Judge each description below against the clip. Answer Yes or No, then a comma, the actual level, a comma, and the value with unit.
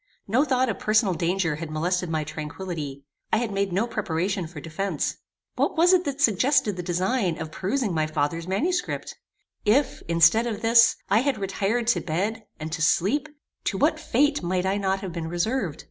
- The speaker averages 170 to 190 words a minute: Yes, average, 185 wpm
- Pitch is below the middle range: No, high, 190 Hz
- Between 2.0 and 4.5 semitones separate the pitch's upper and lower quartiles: No, wide, 5.6 semitones